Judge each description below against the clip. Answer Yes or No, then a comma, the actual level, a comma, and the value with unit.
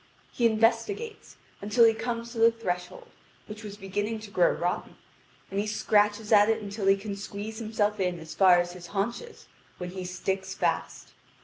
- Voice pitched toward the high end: Yes, high, 205 Hz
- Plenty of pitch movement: No, average, 2.8 semitones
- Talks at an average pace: Yes, average, 180 wpm